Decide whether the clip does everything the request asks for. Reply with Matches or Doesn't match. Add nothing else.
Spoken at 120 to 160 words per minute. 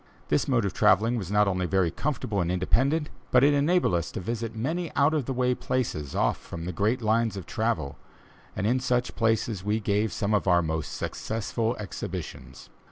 Doesn't match